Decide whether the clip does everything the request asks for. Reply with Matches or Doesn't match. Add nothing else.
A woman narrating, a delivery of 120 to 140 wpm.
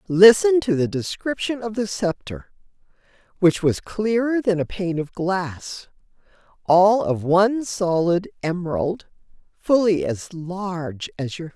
Matches